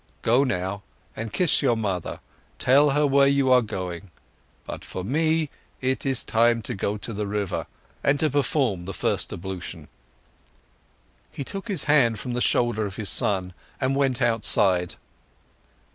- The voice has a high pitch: No, low, 120 Hz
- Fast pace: No, average, 160 wpm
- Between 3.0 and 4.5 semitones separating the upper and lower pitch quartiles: No, wide, 5.6 semitones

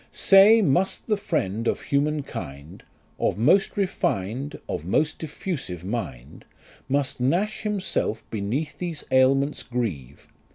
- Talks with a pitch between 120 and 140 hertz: Yes, low, 135 Hz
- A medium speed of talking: No, slow, 125 wpm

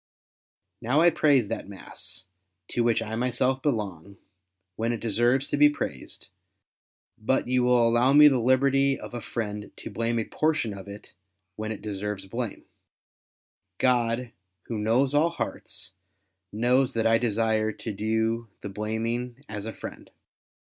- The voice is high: No, low, 115 Hz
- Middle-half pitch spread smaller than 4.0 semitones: Yes, average, 2.8 semitones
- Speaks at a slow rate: No, average, 150 wpm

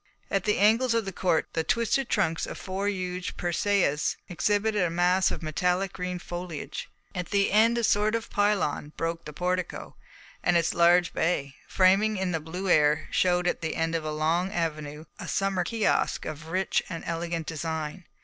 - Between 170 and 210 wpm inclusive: Yes, average, 180 wpm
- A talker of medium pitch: Yes, medium, 180 Hz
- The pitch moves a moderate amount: Yes, average, 3.3 semitones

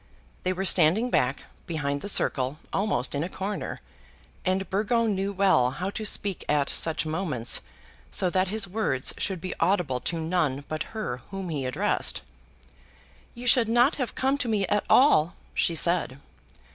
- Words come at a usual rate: Yes, average, 165 wpm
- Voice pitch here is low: No, medium, 185 Hz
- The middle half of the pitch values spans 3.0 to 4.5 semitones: No, average, 5.2 semitones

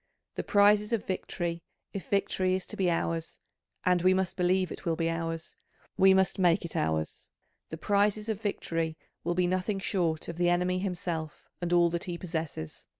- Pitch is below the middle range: No, medium, 180 Hz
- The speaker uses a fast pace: No, average, 185 wpm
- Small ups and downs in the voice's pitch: Yes, narrow, 2.3 semitones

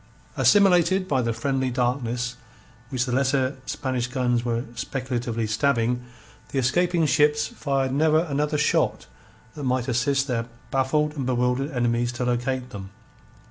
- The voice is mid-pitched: No, low, 130 Hz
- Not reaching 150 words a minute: Yes, average, 140 wpm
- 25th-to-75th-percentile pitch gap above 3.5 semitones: No, average, 2.7 semitones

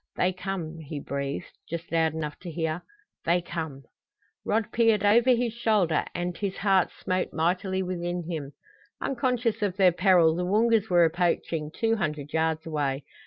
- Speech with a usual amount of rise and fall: Yes, average, 4.1 semitones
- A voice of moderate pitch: Yes, medium, 175 Hz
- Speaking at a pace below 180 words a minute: Yes, average, 160 wpm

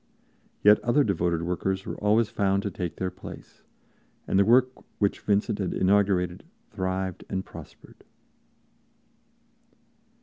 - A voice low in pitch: Yes, very low, 95 Hz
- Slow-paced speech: Yes, slow, 125 wpm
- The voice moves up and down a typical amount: No, narrow, 1.9 semitones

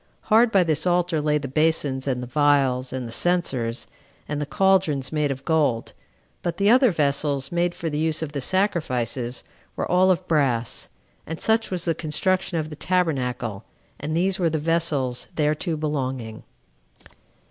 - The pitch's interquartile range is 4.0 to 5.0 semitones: Yes, average, 4.6 semitones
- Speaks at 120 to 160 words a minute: No, average, 170 wpm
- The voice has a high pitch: No, medium, 150 Hz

